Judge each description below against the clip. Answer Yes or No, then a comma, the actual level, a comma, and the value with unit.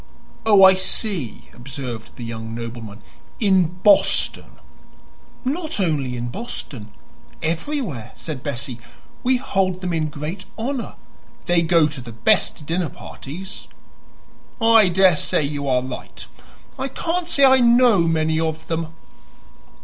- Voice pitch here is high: No, medium, 165 Hz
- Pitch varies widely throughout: Yes, wide, 7.5 semitones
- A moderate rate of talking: No, slow, 125 wpm